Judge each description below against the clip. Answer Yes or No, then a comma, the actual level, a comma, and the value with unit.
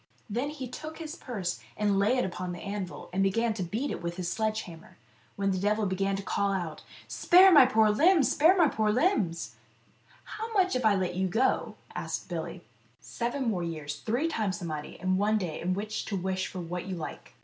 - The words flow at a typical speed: No, fast, 235 wpm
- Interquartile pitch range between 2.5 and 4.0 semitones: No, wide, 5.4 semitones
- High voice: Yes, high, 205 Hz